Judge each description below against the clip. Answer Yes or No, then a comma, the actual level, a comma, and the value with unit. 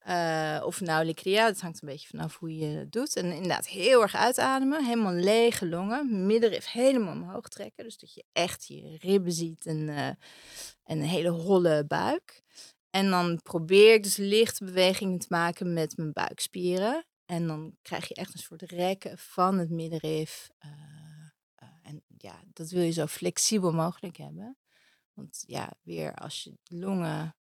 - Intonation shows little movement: No, average, 3.8 semitones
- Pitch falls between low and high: Yes, medium, 175 Hz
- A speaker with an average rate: Yes, average, 170 wpm